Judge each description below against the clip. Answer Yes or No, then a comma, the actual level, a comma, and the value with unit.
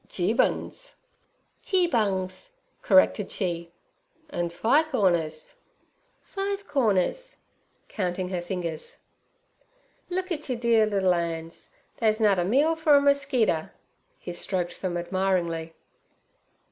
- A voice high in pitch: Yes, high, 195 Hz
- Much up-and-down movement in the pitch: Yes, wide, 8.2 semitones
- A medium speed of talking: No, slow, 105 wpm